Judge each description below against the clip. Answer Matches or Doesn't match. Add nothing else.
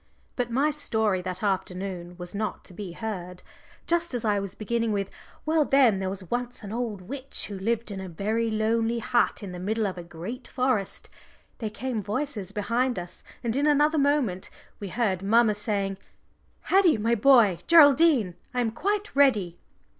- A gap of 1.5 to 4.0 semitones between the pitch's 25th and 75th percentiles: Doesn't match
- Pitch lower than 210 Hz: Doesn't match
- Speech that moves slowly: Doesn't match